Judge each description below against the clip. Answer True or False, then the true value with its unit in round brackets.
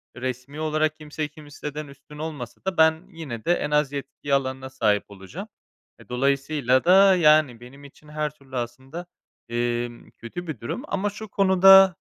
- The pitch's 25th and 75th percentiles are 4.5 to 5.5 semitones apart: False (3.7 semitones)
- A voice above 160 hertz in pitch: False (145 Hz)